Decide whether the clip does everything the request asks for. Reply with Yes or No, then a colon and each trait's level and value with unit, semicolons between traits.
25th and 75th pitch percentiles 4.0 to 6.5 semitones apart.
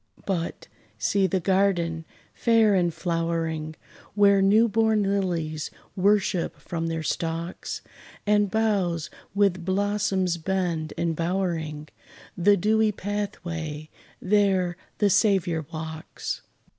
No: average, 3.6 semitones